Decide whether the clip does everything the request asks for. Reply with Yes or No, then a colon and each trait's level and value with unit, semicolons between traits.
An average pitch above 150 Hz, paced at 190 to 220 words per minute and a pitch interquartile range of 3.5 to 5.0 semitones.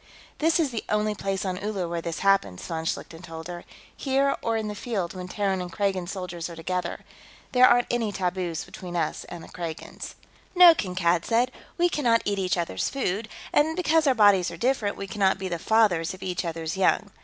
Yes: high, 190 Hz; fast, 205 wpm; average, 4.6 semitones